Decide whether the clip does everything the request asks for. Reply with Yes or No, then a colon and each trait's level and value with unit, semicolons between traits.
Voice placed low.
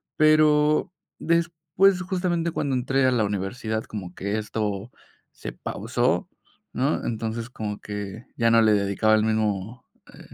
Yes: low, 115 Hz